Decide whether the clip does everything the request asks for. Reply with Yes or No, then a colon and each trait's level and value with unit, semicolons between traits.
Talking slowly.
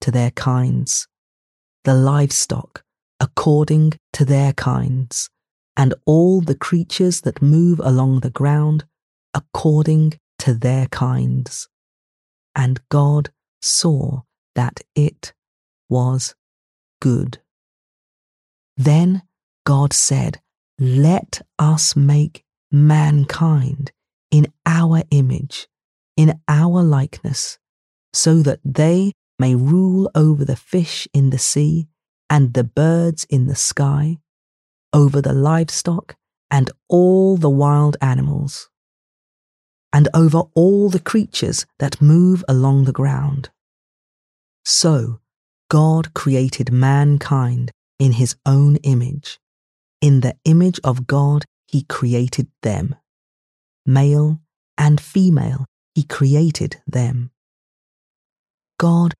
Yes: slow, 100 wpm